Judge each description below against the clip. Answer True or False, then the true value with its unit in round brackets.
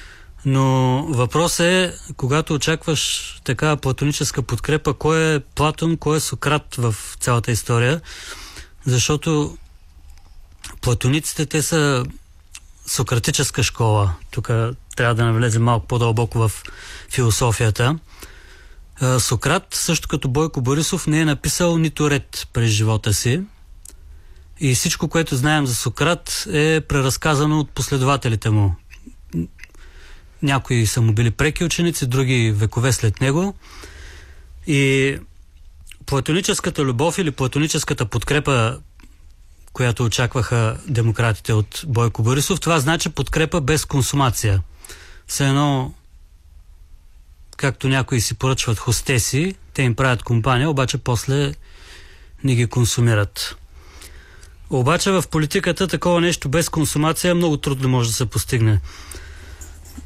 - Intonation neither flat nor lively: False (6.7 semitones)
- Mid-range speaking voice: False (125 Hz)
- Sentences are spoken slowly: True (110 wpm)